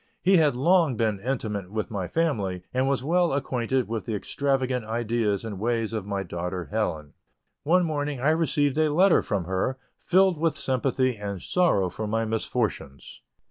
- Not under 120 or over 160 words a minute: No, average, 170 wpm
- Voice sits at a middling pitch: No, low, 120 Hz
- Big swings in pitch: Yes, wide, 6.0 semitones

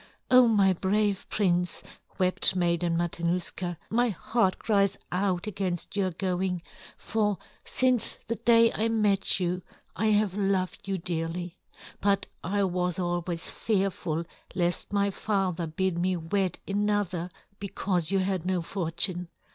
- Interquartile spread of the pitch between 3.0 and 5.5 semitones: No, narrow, 2.5 semitones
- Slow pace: Yes, slow, 130 wpm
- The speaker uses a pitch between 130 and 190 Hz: Yes, medium, 185 Hz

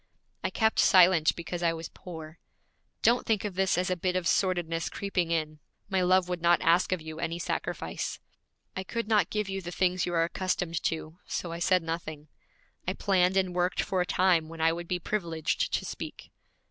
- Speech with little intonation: Yes, narrow, 2.1 semitones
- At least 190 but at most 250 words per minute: Yes, average, 200 wpm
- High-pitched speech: No, medium, 175 Hz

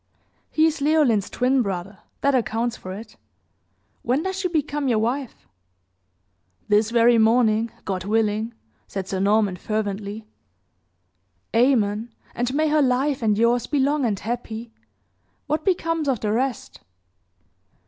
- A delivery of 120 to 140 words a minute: Yes, slow, 135 wpm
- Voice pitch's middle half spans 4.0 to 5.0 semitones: Yes, average, 4.5 semitones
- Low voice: No, high, 235 Hz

